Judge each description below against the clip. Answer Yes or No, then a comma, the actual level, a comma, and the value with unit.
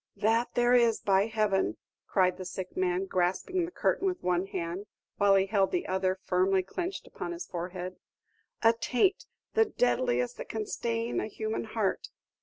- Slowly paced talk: No, average, 170 wpm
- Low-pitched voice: No, high, 205 Hz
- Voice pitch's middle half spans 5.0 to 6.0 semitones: No, average, 4.2 semitones